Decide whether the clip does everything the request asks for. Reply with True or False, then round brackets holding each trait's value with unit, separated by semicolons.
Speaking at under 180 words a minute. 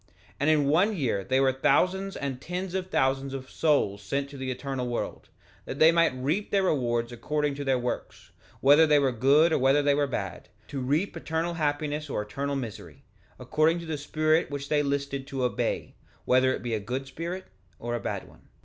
False (205 wpm)